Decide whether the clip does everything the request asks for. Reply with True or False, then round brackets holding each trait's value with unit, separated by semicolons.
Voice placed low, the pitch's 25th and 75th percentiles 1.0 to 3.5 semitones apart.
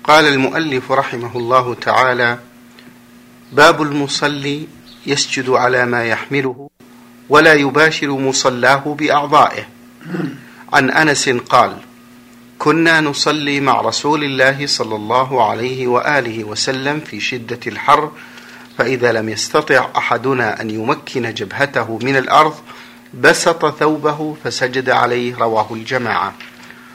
True (130 Hz; 3.2 semitones)